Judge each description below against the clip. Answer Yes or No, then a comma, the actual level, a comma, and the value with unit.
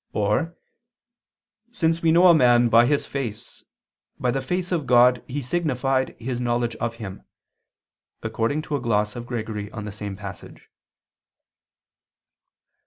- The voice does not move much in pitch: No, average, 4.2 semitones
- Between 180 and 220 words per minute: No, average, 140 wpm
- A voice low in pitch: Yes, low, 120 Hz